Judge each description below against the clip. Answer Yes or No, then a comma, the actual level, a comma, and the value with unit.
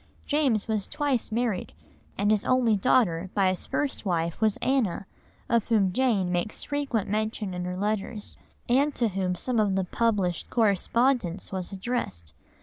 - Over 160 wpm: No, average, 155 wpm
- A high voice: Yes, high, 210 Hz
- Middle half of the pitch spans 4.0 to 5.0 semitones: Yes, average, 4.4 semitones